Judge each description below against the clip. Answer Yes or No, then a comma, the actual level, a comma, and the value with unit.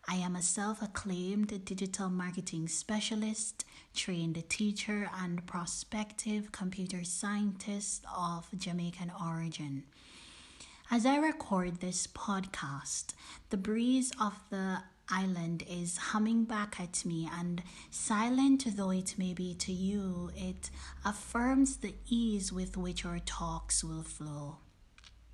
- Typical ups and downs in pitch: Yes, average, 3.2 semitones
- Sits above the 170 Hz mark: Yes, medium, 185 Hz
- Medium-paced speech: No, slow, 120 wpm